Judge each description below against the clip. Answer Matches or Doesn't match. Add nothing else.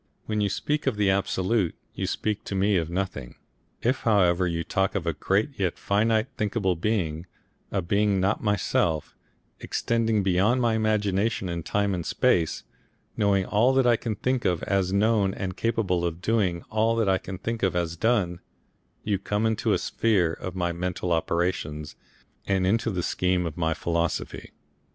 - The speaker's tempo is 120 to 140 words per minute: Doesn't match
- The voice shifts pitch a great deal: Doesn't match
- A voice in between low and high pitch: Doesn't match